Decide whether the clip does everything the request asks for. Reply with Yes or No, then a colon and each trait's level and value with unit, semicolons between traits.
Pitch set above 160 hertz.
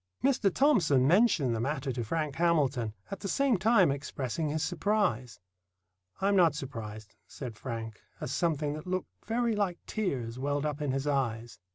No: medium, 150 Hz